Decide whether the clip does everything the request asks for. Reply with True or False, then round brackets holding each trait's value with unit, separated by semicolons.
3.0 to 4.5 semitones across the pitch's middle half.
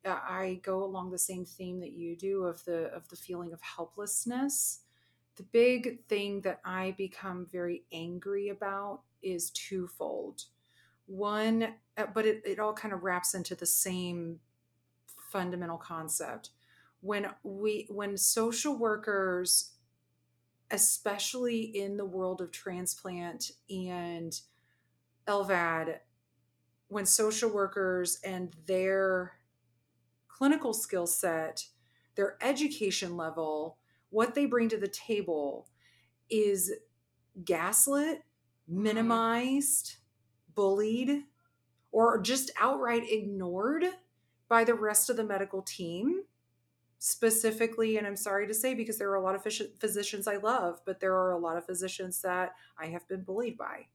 True (3.9 semitones)